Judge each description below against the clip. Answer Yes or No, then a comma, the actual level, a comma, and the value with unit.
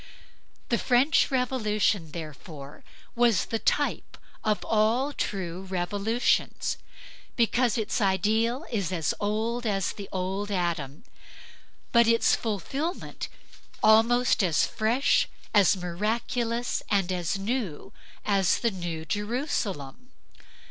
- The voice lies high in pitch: Yes, high, 210 Hz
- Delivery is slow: Yes, slow, 105 wpm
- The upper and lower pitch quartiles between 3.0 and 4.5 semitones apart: Yes, average, 4.2 semitones